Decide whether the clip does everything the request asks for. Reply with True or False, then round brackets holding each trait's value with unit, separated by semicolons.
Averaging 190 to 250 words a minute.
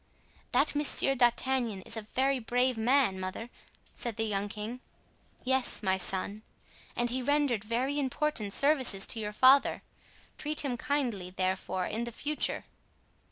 False (145 wpm)